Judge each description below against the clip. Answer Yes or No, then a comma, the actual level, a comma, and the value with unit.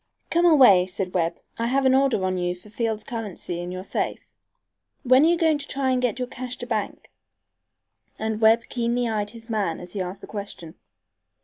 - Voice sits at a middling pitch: No, high, 225 Hz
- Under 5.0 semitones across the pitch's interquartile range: No, average, 5.3 semitones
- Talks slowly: No, fast, 205 wpm